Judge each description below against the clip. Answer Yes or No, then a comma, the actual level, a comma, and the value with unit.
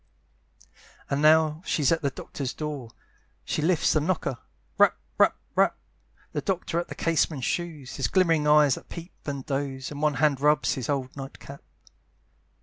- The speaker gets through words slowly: No, average, 165 wpm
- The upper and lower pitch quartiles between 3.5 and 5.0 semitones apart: No, narrow, 2.6 semitones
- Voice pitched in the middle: Yes, medium, 150 Hz